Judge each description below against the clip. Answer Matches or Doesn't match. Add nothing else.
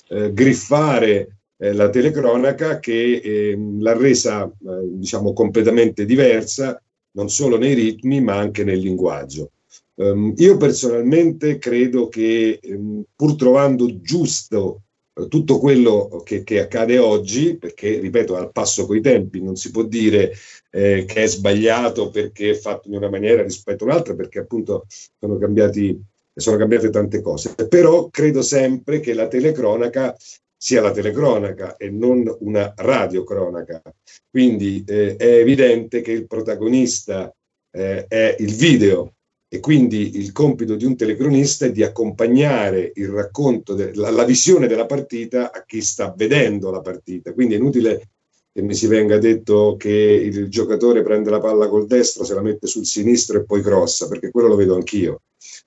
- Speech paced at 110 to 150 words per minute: Matches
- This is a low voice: Matches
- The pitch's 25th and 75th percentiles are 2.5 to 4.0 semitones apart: Matches